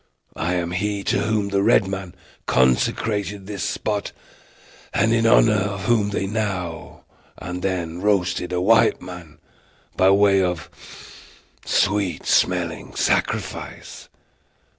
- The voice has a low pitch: Yes, very low, 95 Hz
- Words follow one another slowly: Yes, slow, 120 wpm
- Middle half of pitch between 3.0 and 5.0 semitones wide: No, narrow, 2.5 semitones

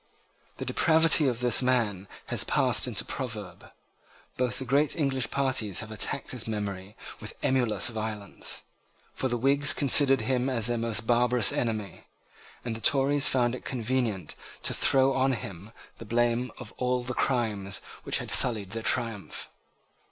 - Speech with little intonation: No, average, 3.3 semitones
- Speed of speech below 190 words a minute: Yes, average, 160 wpm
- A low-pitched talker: Yes, low, 120 Hz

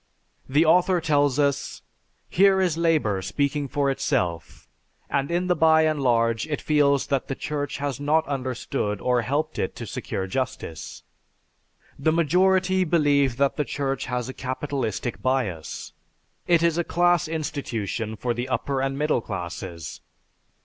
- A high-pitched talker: No, medium, 140 Hz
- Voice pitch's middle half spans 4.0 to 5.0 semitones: Yes, average, 4.3 semitones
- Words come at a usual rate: Yes, average, 150 wpm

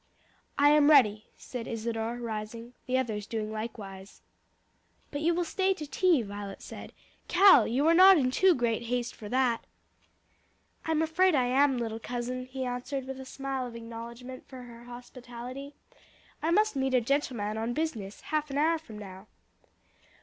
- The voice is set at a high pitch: Yes, very high, 250 Hz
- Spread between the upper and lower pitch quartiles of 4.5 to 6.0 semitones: No, average, 4.0 semitones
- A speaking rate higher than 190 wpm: No, average, 165 wpm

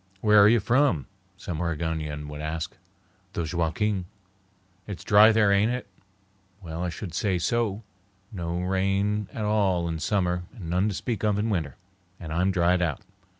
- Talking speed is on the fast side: No, average, 165 wpm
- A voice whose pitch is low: Yes, very low, 95 Hz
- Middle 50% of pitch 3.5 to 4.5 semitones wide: Yes, average, 3.8 semitones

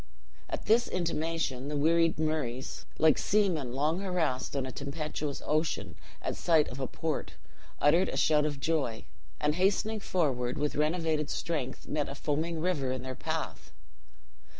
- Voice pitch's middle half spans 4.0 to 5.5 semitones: No, average, 3.2 semitones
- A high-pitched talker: No, medium, 150 Hz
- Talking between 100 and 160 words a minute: Yes, average, 150 wpm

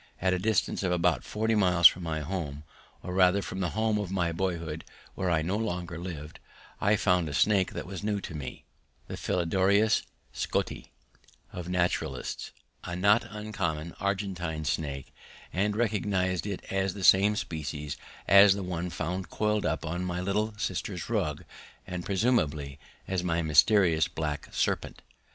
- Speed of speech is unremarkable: Yes, average, 160 wpm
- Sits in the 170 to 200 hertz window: No, very low, 90 Hz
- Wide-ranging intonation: No, average, 3.3 semitones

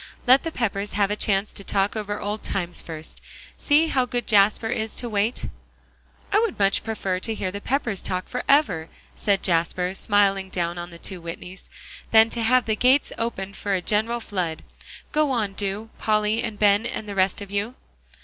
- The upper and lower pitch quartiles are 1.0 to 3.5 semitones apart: Yes, average, 2.9 semitones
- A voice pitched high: Yes, high, 205 Hz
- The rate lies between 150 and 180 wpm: No, average, 190 wpm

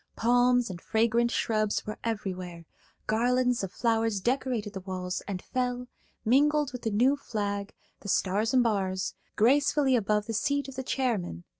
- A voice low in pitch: No, high, 225 Hz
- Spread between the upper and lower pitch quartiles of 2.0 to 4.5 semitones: Yes, average, 3.7 semitones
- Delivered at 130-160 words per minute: Yes, average, 145 wpm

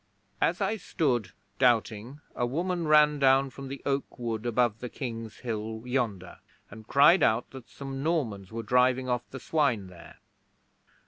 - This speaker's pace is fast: No, average, 155 wpm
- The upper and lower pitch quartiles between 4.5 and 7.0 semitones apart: No, average, 3.7 semitones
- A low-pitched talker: Yes, low, 125 Hz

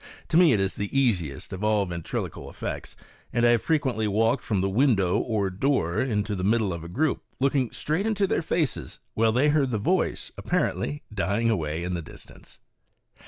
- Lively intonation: Yes, wide, 6.2 semitones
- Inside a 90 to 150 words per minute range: No, average, 195 wpm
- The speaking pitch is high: No, low, 110 Hz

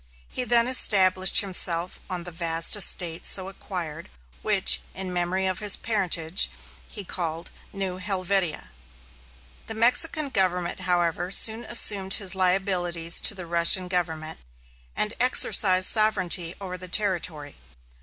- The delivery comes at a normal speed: No, slow, 125 wpm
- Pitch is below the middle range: No, medium, 185 Hz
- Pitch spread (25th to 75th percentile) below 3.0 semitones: Yes, narrow, 2.4 semitones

